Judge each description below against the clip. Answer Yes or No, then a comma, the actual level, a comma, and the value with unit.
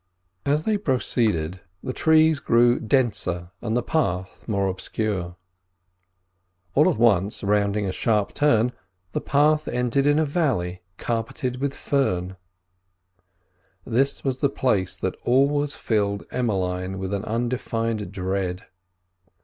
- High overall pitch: No, low, 115 Hz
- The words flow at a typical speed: No, slow, 125 wpm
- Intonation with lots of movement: Yes, wide, 6.0 semitones